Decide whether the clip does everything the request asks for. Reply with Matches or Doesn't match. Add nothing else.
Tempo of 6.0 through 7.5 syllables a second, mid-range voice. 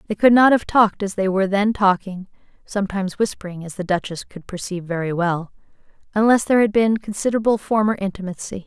Doesn't match